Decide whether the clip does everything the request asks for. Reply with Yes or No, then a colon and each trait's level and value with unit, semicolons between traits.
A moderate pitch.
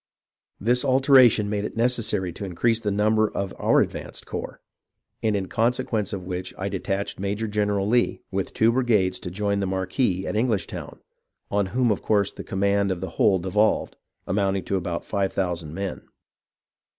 No: low, 100 Hz